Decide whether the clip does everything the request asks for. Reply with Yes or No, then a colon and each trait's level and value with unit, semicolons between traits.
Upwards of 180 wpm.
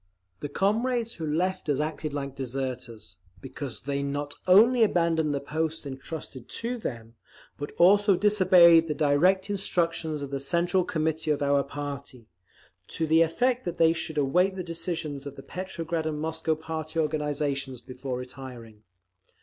No: average, 150 wpm